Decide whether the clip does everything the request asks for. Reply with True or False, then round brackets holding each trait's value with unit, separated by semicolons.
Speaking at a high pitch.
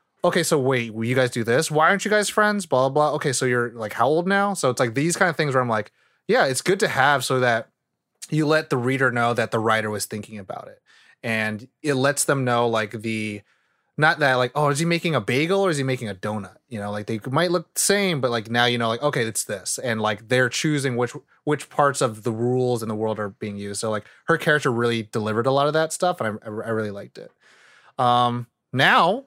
False (125 Hz)